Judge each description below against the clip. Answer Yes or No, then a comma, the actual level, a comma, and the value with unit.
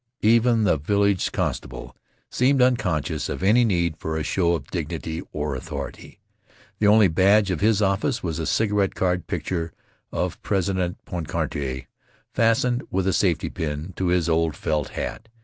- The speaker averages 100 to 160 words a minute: Yes, average, 155 wpm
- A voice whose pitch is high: No, very low, 90 Hz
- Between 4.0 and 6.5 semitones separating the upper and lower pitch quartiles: Yes, average, 4.5 semitones